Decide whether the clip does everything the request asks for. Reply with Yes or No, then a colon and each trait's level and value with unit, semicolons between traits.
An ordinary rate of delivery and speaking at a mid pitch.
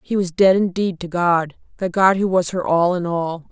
No: fast, 220 wpm; medium, 180 Hz